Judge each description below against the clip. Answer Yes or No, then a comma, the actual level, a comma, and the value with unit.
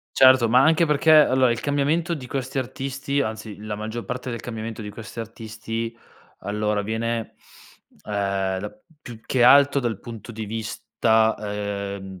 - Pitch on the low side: Yes, low, 115 Hz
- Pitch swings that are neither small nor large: Yes, average, 3.7 semitones